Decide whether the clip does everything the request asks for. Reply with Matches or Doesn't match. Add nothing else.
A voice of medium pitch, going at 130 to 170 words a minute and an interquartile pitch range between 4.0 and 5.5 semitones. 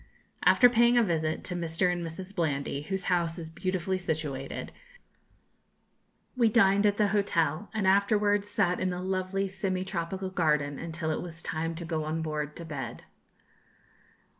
Doesn't match